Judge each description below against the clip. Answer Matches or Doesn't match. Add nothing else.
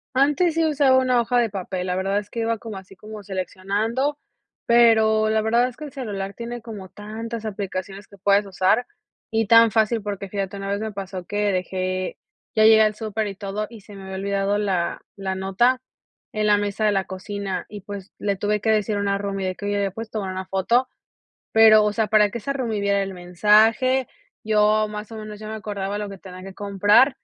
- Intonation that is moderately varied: Doesn't match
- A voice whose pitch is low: Doesn't match